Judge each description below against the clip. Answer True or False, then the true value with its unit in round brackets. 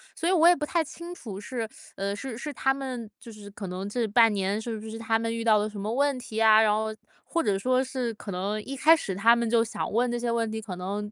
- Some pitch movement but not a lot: True (3.4 semitones)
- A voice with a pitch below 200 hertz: False (225 Hz)